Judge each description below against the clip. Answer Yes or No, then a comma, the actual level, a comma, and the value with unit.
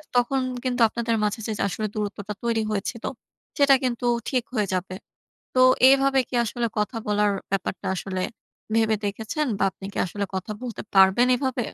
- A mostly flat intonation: No, average, 3.5 semitones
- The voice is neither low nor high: No, high, 225 Hz